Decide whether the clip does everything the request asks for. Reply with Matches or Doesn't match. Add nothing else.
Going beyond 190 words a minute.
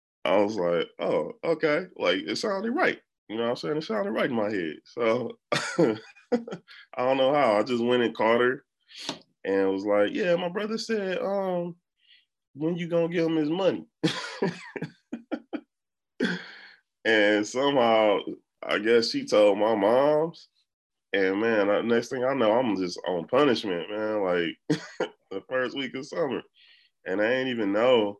Doesn't match